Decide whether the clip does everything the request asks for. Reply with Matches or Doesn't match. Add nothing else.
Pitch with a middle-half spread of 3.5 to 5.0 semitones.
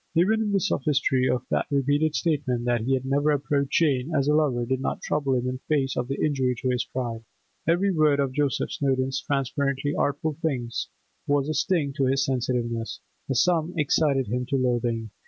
Doesn't match